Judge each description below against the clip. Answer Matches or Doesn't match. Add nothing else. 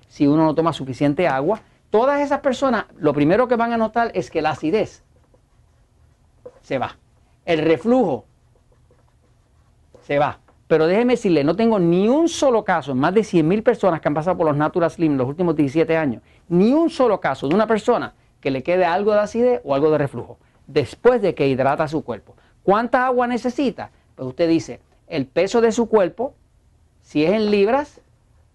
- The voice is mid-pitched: Matches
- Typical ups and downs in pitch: Doesn't match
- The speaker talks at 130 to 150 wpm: Doesn't match